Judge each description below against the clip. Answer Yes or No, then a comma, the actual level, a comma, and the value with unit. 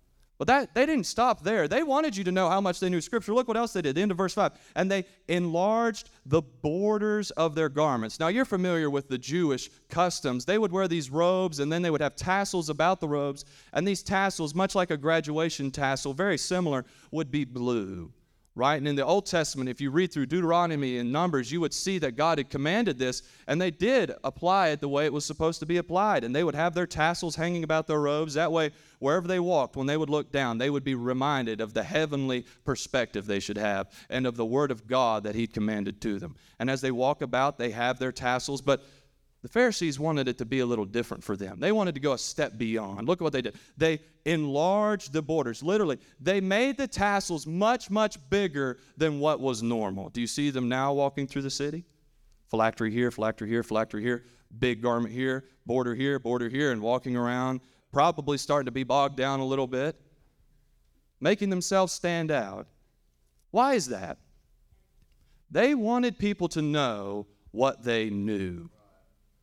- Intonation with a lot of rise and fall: Yes, wide, 5.7 semitones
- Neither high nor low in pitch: Yes, medium, 145 Hz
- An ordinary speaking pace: No, fast, 210 wpm